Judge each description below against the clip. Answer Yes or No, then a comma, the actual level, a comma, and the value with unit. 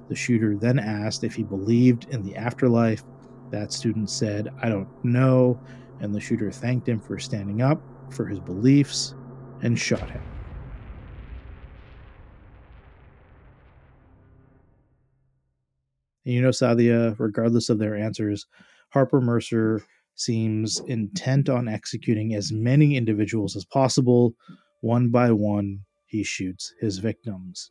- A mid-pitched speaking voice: No, low, 115 Hz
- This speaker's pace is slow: Yes, slow, 120 wpm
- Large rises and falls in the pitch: No, average, 3.1 semitones